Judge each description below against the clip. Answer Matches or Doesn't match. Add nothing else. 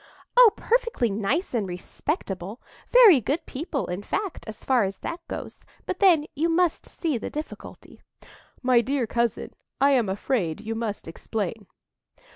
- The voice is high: Matches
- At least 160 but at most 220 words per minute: Doesn't match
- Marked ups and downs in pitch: Matches